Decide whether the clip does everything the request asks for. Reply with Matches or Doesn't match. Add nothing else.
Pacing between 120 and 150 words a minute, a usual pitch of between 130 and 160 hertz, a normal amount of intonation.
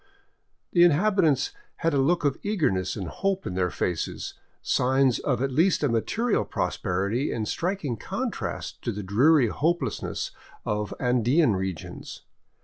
Doesn't match